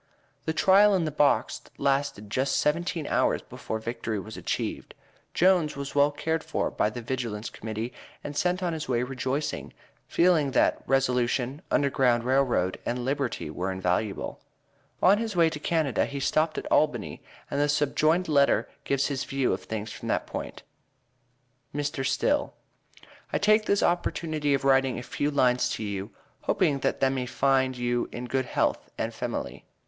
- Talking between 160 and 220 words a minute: Yes, average, 170 wpm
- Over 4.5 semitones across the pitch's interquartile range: No, average, 4.0 semitones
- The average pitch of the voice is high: No, low, 135 Hz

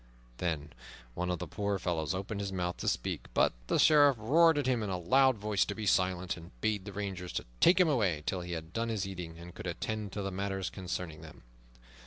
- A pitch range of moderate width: Yes, average, 3.5 semitones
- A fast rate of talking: Yes, fast, 230 wpm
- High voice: No, very low, 95 Hz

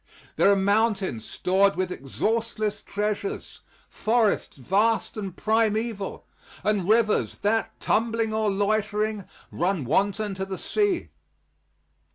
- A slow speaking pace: Yes, slow, 110 wpm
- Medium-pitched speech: No, high, 210 Hz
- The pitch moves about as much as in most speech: No, narrow, 2.2 semitones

